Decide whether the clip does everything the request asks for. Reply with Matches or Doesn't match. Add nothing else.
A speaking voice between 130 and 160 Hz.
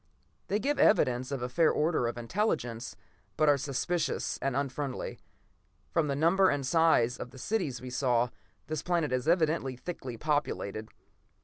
Matches